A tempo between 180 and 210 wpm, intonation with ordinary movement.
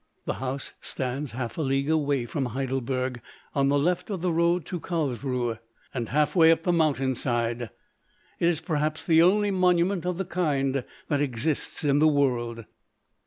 No: average, 170 wpm; average, 4.5 semitones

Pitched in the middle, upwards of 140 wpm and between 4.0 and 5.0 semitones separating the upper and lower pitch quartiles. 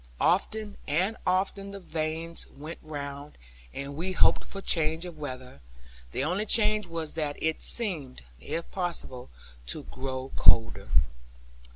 No: medium, 160 Hz; slow, 135 wpm; average, 4.7 semitones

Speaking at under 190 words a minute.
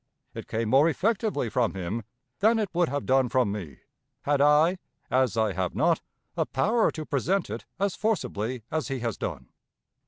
Yes: average, 180 wpm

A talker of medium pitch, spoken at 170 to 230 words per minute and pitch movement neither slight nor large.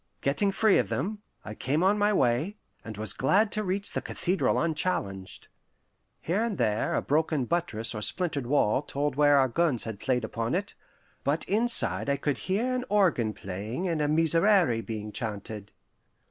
No: medium, 145 Hz; average, 175 wpm; wide, 8.6 semitones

